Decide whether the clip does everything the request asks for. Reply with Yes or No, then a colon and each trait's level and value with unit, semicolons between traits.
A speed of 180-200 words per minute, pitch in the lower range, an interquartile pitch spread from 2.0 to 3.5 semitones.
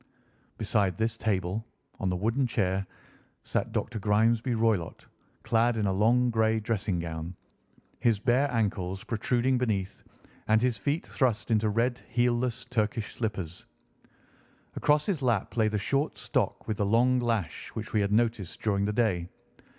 No: average, 150 wpm; low, 110 Hz; average, 3.2 semitones